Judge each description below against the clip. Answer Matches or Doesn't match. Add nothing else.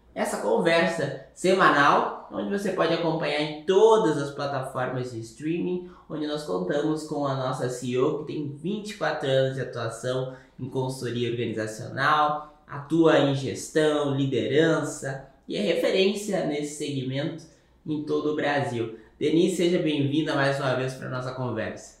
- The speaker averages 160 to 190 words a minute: Doesn't match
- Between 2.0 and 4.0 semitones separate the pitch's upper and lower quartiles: Matches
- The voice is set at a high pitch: Doesn't match